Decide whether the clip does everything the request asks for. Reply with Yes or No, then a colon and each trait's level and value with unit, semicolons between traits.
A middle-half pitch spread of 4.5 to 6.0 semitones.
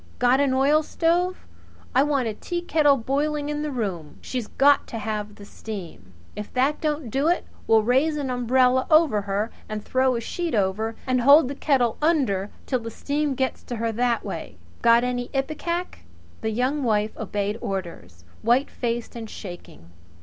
Yes: average, 5.0 semitones